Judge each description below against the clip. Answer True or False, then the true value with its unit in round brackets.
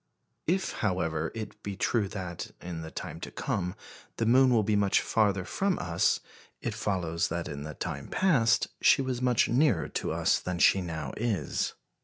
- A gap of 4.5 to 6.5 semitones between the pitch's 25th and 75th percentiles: True (5.3 semitones)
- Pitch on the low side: True (100 Hz)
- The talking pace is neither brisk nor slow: True (180 wpm)